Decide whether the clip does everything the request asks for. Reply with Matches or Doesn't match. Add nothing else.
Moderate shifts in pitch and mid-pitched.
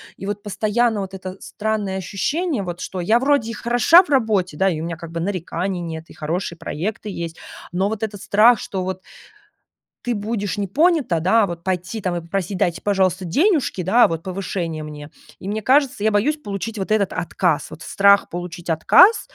Doesn't match